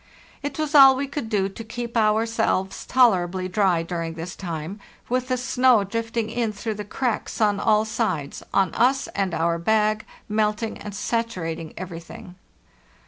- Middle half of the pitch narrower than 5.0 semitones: Yes, average, 4.0 semitones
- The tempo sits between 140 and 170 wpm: Yes, average, 160 wpm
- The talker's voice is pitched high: Yes, high, 215 Hz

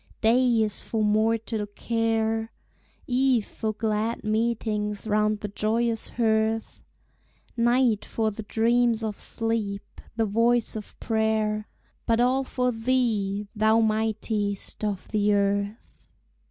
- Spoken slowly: Yes, slow, 115 wpm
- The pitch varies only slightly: Yes, narrow, 1.5 semitones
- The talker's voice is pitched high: Yes, high, 220 Hz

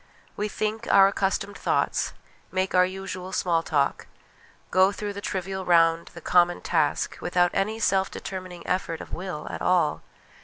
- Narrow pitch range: Yes, narrow, 1.9 semitones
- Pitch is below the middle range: No, medium, 185 Hz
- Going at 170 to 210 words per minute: No, average, 155 wpm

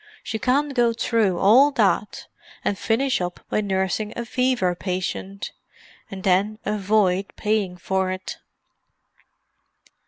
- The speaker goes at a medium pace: No, slow, 115 wpm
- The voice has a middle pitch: No, high, 205 Hz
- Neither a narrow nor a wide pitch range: Yes, average, 3.5 semitones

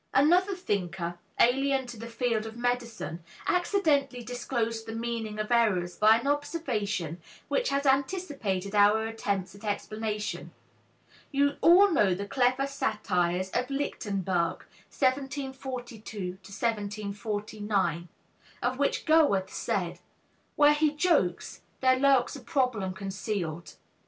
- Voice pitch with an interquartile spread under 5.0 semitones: No, average, 5.3 semitones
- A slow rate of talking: Yes, slow, 115 wpm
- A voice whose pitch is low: No, high, 230 Hz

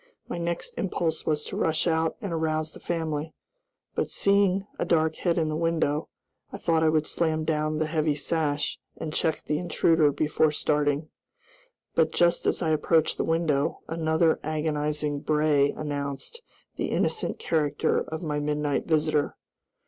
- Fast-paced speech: No, average, 155 wpm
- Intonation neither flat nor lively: No, narrow, 1.5 semitones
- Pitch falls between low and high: Yes, medium, 155 Hz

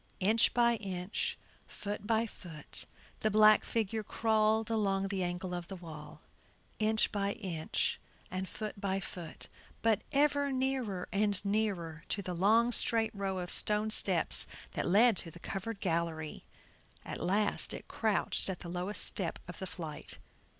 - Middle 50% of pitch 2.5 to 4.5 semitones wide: Yes, average, 3.5 semitones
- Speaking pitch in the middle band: No, high, 200 Hz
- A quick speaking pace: No, average, 155 wpm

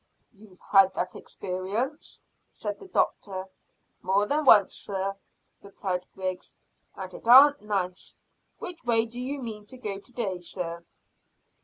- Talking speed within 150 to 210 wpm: No, slow, 135 wpm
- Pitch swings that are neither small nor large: Yes, average, 4.3 semitones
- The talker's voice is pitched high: Yes, high, 200 Hz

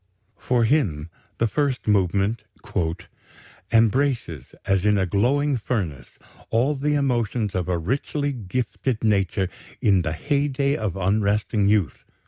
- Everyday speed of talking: No, slow, 120 wpm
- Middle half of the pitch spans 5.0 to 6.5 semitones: Yes, average, 5.3 semitones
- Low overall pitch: Yes, low, 110 Hz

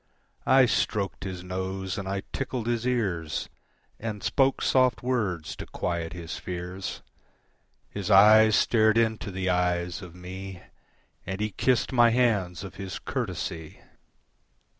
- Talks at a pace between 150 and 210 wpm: No, slow, 135 wpm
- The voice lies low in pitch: Yes, very low, 95 Hz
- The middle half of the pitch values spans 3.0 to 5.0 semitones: Yes, average, 4.0 semitones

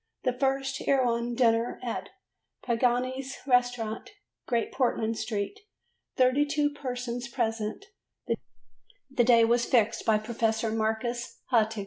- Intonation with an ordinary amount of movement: No, narrow, 2.2 semitones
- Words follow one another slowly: Yes, slow, 105 wpm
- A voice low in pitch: No, high, 240 Hz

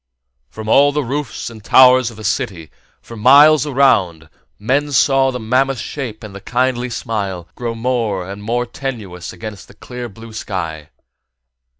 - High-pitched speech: No, low, 115 Hz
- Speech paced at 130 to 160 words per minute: No, average, 175 wpm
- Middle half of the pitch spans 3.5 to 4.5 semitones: Yes, average, 4.1 semitones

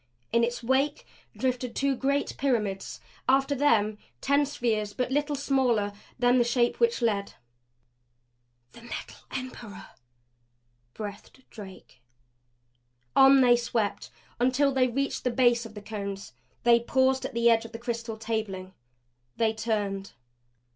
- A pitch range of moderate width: Yes, average, 3.4 semitones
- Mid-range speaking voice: No, high, 235 Hz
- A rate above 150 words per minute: No, slow, 135 wpm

